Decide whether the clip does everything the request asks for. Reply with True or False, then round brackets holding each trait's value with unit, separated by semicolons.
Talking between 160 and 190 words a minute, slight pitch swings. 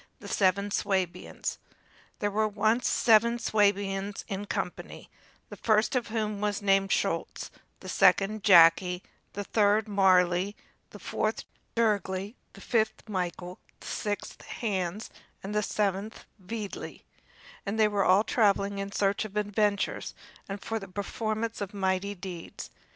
False (135 wpm; 1.8 semitones)